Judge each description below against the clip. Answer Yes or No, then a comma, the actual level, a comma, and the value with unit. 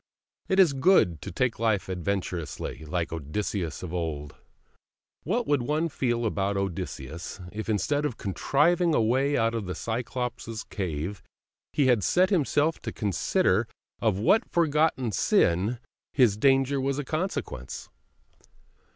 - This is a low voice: Yes, low, 115 Hz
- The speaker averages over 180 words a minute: No, slow, 135 wpm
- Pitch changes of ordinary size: No, wide, 7.5 semitones